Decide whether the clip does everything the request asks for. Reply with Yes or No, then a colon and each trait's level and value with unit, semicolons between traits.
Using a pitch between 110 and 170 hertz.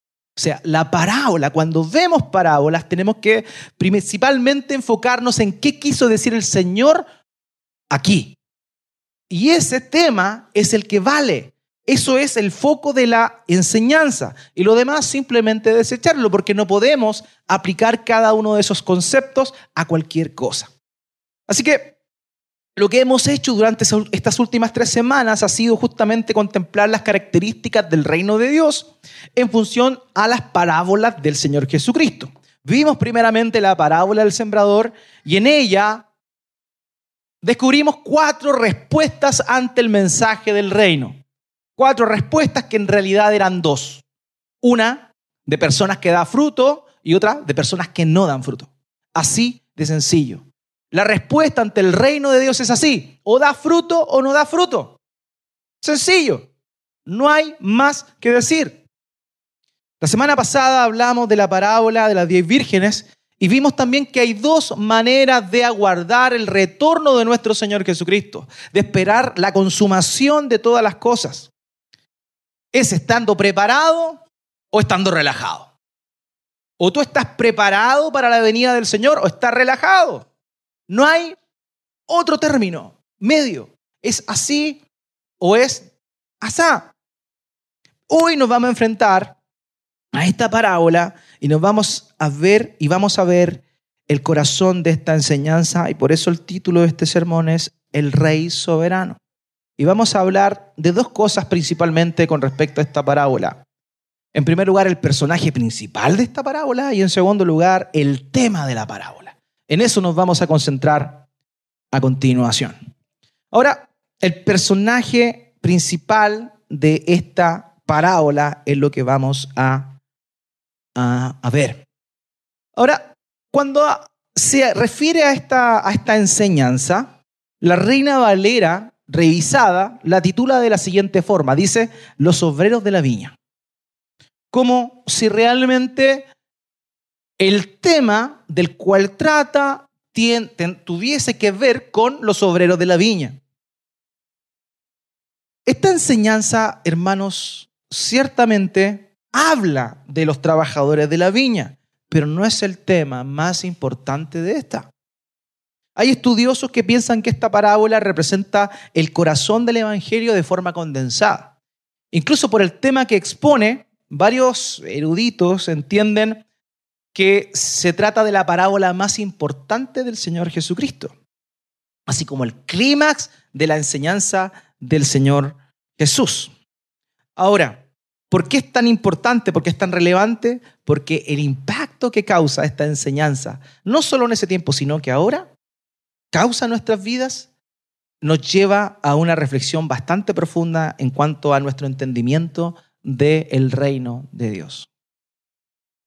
No: high, 200 Hz